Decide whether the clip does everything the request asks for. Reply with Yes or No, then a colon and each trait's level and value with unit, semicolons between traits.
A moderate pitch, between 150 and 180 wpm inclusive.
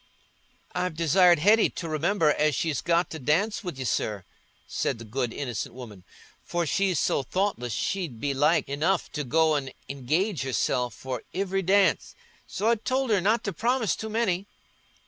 Yes: medium, 165 Hz; average, 170 wpm